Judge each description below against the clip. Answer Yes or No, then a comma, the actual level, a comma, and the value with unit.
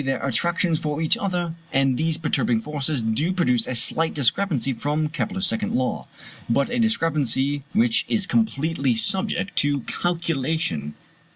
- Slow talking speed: No, average, 145 wpm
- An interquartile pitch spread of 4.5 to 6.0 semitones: Yes, average, 4.9 semitones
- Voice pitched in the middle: Yes, medium, 155 Hz